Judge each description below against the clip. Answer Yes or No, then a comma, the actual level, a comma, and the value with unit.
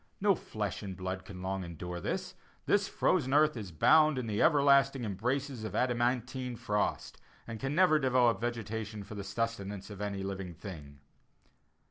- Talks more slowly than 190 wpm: Yes, average, 160 wpm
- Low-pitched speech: Yes, low, 115 Hz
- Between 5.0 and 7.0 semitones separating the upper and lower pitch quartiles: Yes, wide, 5.4 semitones